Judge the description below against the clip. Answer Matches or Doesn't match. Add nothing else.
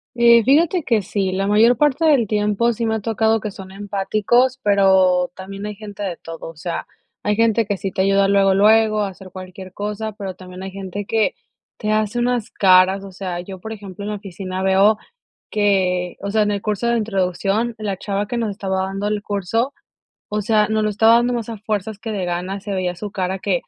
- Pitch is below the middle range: Doesn't match